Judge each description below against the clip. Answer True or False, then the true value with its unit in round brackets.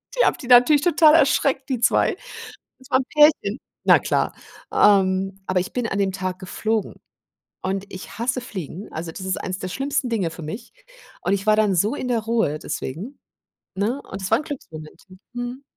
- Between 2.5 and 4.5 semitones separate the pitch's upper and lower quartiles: False (5.4 semitones)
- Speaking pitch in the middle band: False (215 Hz)